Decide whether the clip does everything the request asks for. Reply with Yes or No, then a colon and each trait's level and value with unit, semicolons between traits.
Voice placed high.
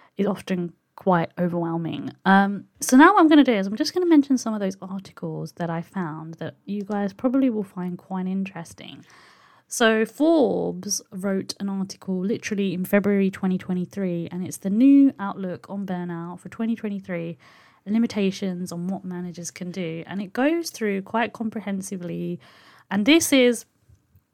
Yes: high, 195 Hz